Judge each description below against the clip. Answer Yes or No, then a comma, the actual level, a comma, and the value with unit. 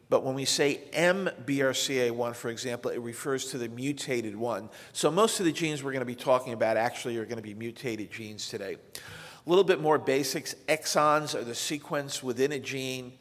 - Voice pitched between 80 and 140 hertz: Yes, low, 135 Hz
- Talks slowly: No, average, 200 wpm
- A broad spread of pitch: No, average, 3.9 semitones